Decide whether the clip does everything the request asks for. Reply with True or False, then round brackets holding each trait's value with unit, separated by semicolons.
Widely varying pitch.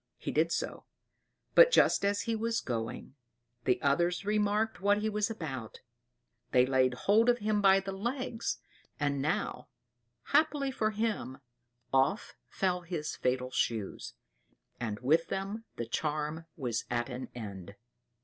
True (8.8 semitones)